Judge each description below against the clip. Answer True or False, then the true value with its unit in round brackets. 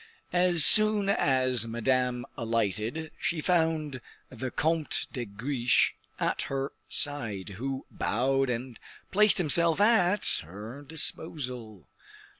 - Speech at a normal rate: False (105 wpm)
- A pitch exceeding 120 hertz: True (135 Hz)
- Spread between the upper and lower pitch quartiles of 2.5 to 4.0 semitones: False (5.5 semitones)